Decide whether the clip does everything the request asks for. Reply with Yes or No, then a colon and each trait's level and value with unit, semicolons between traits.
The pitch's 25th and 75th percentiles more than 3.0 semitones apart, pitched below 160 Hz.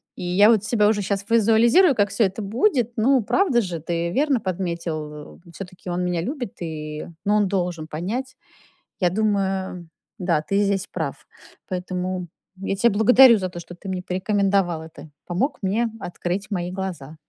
No: average, 3.7 semitones; high, 190 Hz